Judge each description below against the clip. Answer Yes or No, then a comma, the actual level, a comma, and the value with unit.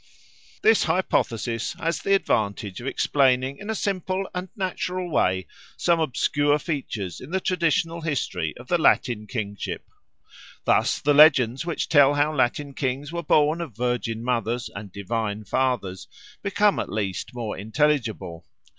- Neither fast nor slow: Yes, average, 145 wpm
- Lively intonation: Yes, wide, 6.8 semitones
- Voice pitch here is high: No, low, 135 Hz